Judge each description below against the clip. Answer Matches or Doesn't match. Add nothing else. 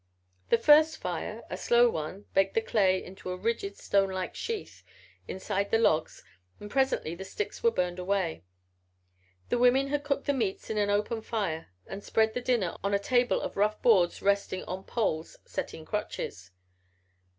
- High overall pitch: Matches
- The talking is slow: Doesn't match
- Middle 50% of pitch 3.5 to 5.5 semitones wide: Matches